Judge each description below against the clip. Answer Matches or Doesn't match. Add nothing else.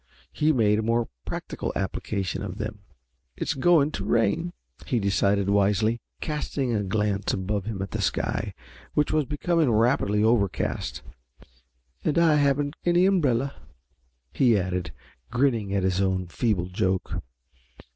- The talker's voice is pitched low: Matches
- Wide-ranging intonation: Matches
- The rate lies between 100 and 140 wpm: Matches